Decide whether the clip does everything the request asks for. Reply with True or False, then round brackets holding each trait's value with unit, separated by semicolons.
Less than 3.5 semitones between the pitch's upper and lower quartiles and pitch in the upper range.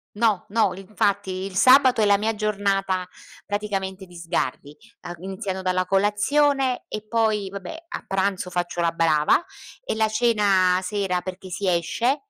True (2.8 semitones; 195 Hz)